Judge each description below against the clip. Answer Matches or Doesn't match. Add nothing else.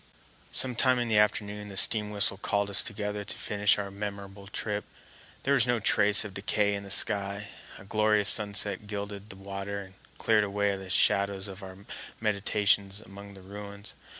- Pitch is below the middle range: Matches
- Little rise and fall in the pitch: Matches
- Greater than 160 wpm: Matches